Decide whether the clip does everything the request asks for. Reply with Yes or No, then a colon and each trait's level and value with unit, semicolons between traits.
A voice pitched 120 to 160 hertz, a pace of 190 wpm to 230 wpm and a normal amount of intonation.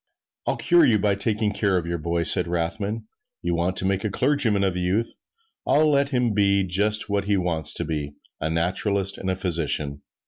No: very low, 95 Hz; fast, 205 wpm; average, 3.7 semitones